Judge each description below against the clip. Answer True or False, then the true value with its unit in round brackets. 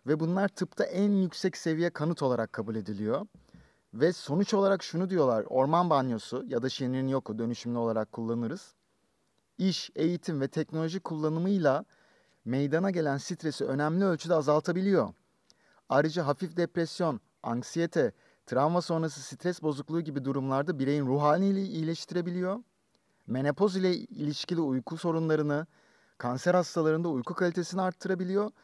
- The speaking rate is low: False (120 wpm)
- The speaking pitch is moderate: True (160 Hz)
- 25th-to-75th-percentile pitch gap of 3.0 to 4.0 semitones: False (4.5 semitones)